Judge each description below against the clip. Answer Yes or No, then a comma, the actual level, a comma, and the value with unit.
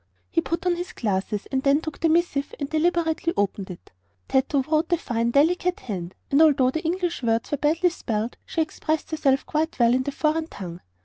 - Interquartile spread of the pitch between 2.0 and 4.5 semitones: No, wide, 5.4 semitones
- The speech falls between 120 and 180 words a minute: No, average, 200 wpm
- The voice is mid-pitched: No, very high, 300 Hz